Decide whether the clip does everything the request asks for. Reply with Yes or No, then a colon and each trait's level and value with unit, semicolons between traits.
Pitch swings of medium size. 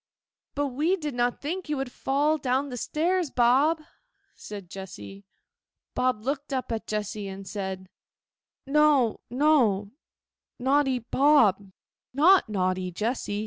No: wide, 5.9 semitones